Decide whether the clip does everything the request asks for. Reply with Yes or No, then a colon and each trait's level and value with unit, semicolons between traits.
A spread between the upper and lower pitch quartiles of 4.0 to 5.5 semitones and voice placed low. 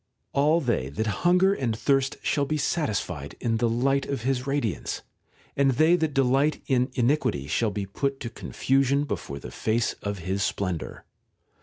Yes: average, 4.3 semitones; low, 130 Hz